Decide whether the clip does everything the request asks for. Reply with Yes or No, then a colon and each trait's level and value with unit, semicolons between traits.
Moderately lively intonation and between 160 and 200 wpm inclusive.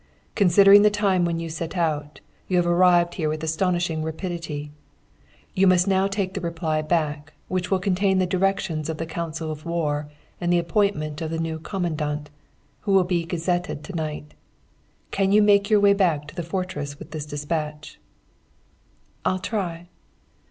Yes: average, 3.3 semitones; average, 170 wpm